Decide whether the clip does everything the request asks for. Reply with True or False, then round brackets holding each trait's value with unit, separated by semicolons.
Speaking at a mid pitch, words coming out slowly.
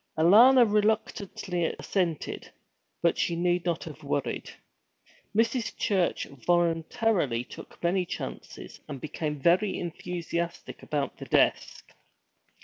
True (175 Hz; 105 wpm)